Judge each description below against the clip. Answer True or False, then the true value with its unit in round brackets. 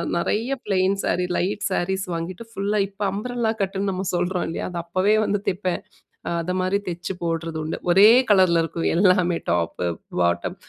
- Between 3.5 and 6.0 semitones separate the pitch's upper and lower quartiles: False (2.7 semitones)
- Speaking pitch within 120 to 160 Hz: False (185 Hz)